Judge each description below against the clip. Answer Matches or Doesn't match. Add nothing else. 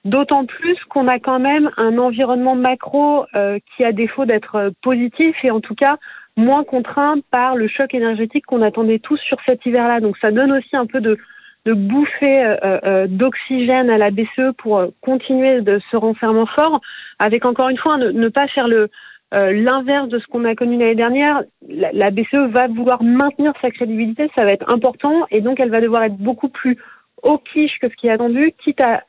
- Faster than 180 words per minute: Matches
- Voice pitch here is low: Doesn't match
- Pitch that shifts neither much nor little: Matches